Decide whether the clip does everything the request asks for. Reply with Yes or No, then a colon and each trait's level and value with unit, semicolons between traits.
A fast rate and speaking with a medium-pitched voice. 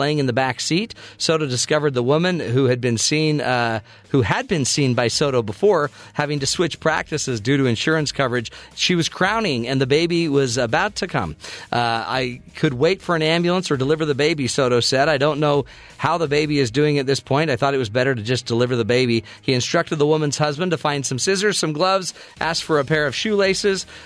Yes: fast, 225 wpm; medium, 145 Hz